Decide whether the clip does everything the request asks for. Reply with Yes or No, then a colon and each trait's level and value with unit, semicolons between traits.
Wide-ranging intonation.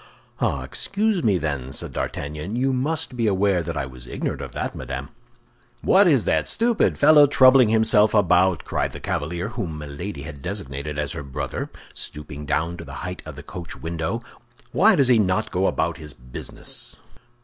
Yes: wide, 7.9 semitones